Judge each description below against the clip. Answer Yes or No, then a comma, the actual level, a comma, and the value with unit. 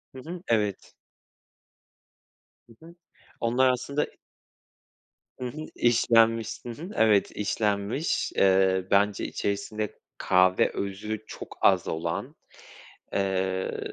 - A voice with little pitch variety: No, average, 3.8 semitones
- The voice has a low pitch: Yes, low, 105 Hz